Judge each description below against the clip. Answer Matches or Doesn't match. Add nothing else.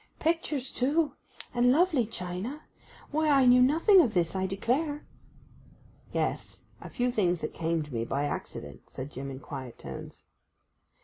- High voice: Matches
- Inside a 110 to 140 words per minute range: Matches